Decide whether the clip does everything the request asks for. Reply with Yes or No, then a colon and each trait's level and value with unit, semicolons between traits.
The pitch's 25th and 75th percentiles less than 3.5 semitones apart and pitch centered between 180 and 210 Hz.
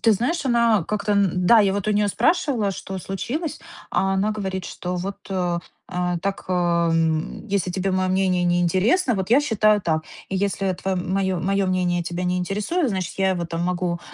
Yes: narrow, 2.4 semitones; high, 190 Hz